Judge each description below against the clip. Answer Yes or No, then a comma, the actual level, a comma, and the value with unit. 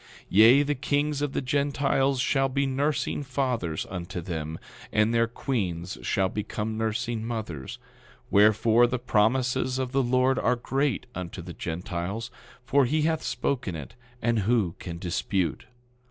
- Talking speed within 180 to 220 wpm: No, average, 150 wpm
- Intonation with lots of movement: Yes, wide, 5.8 semitones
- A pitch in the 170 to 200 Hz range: No, low, 120 Hz